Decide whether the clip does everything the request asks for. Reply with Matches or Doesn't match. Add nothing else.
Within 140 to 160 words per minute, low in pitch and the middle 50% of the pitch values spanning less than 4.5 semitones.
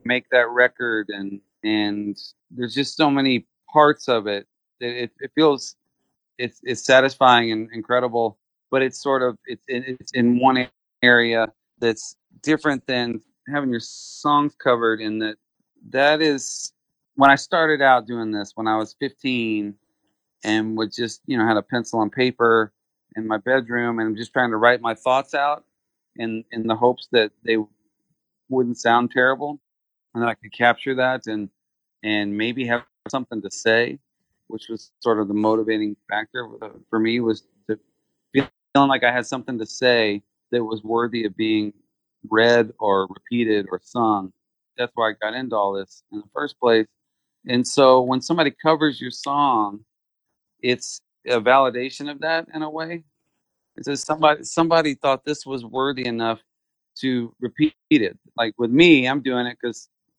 Doesn't match